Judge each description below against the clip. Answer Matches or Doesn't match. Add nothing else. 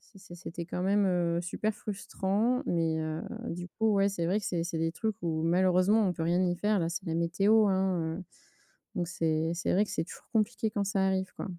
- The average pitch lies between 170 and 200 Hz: Matches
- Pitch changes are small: Doesn't match